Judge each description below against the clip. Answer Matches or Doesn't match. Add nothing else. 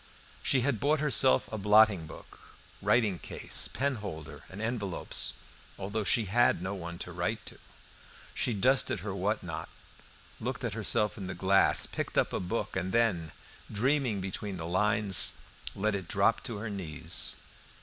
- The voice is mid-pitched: Doesn't match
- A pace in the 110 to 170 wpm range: Matches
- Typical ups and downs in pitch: Matches